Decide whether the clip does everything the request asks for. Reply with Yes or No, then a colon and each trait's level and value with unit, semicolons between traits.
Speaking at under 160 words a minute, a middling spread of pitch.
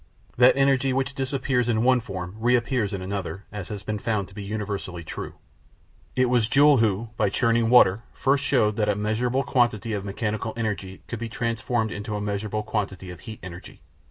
No: average, 185 wpm; average, 3.4 semitones